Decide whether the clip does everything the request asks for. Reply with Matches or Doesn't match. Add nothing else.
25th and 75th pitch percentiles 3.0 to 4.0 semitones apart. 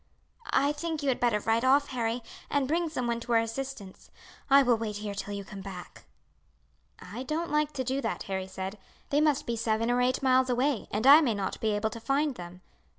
Doesn't match